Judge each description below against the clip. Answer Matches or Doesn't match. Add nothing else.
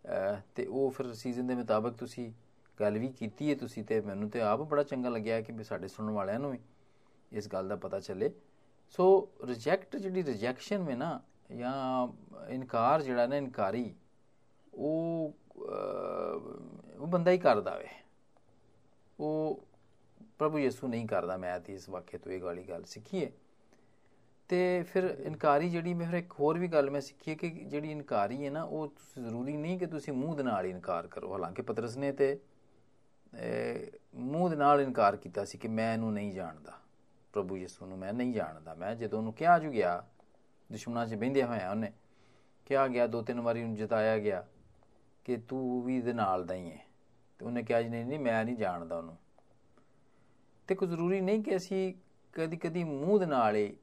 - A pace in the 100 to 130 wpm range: Doesn't match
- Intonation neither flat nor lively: Doesn't match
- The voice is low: Matches